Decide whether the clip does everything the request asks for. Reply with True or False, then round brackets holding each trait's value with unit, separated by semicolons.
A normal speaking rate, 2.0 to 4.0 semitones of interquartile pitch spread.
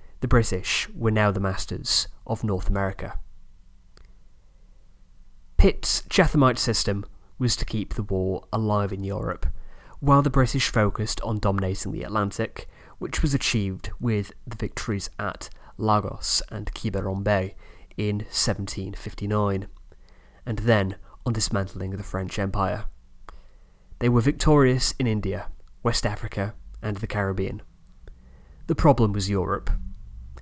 False (120 wpm; 2.9 semitones)